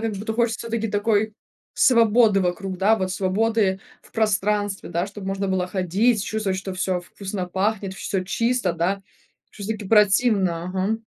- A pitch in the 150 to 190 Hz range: No, high, 200 Hz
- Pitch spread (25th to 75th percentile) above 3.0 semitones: No, narrow, 2.6 semitones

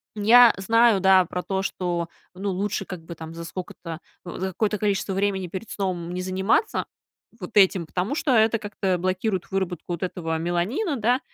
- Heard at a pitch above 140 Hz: Yes, high, 190 Hz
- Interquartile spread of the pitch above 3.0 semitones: No, average, 2.7 semitones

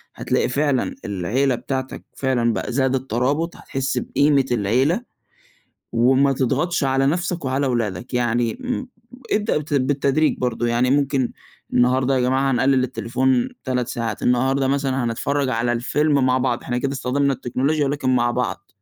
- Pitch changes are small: Yes, narrow, 2.3 semitones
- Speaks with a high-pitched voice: No, low, 130 Hz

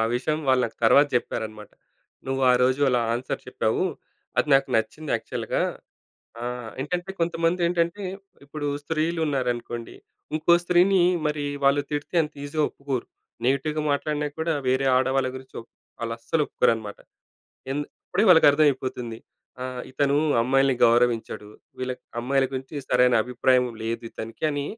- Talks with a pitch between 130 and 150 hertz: Yes, low, 135 Hz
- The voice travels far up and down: No, average, 3.4 semitones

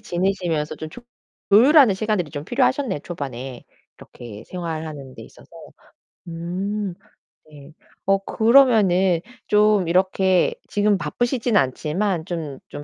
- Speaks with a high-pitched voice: No, medium, 180 Hz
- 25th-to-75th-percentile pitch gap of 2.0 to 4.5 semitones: No, average, 5.1 semitones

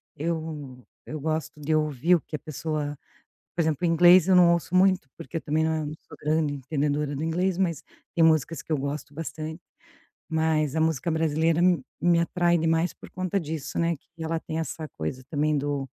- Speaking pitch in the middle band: Yes, medium, 160 Hz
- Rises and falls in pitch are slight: Yes, narrow, 2.1 semitones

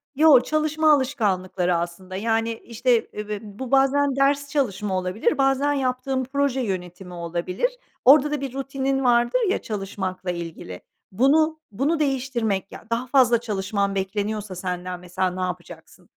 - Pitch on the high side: Yes, high, 230 Hz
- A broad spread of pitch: Yes, wide, 6.4 semitones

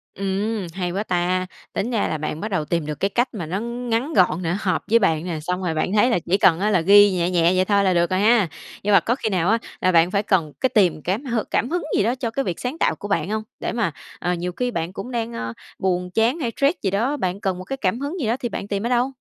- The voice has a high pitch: Yes, high, 195 Hz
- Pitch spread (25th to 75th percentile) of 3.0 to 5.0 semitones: Yes, average, 4.5 semitones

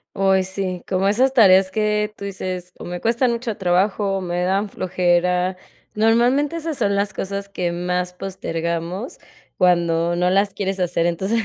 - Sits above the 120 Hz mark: Yes, high, 190 Hz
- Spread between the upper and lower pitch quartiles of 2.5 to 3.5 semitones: Yes, average, 2.8 semitones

